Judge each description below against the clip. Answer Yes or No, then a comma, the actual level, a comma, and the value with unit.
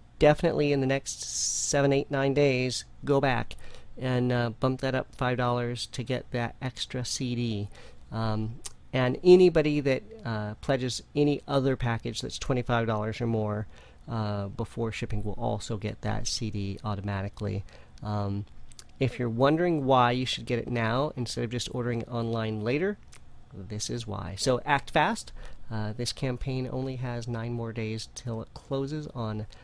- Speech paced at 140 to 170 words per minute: Yes, average, 155 wpm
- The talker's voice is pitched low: Yes, low, 120 Hz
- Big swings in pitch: No, average, 3.3 semitones